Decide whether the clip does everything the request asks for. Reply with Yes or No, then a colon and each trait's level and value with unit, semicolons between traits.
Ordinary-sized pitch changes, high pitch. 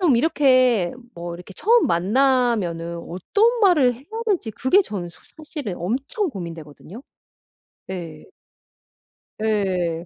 No: wide, 8.2 semitones; high, 220 Hz